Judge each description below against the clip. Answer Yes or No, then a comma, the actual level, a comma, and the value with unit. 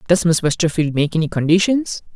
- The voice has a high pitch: No, medium, 170 Hz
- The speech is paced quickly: No, average, 165 wpm